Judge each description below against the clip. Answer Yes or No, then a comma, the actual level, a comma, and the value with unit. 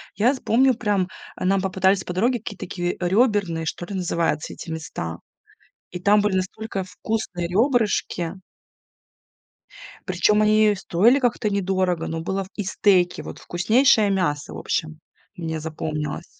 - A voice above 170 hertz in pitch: Yes, high, 190 Hz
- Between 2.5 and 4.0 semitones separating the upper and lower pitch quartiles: Yes, average, 3.4 semitones